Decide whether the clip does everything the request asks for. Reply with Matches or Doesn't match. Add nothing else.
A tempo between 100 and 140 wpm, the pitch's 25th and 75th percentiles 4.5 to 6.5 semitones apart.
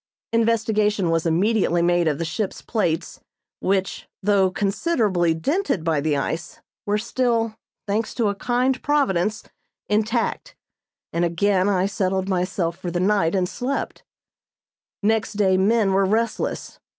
Doesn't match